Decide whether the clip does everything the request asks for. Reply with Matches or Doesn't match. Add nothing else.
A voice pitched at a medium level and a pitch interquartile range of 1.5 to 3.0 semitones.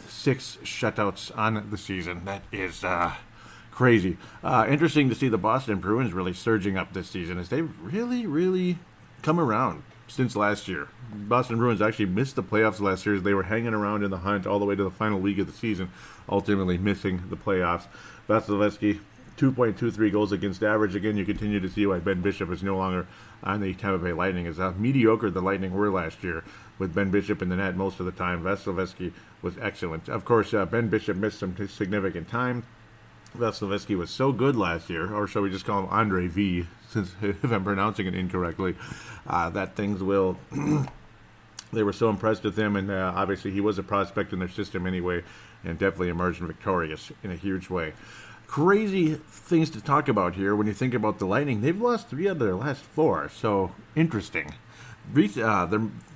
Doesn't match